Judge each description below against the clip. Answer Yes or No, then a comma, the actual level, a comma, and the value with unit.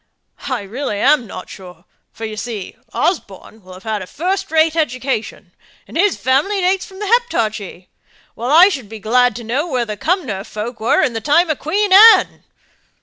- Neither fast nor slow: Yes, average, 190 wpm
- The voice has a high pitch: Yes, very high, 255 Hz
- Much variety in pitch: Yes, wide, 8.2 semitones